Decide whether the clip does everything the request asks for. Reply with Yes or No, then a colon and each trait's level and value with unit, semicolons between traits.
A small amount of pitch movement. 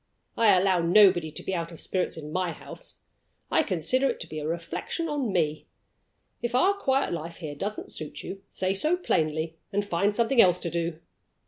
No: average, 4.8 semitones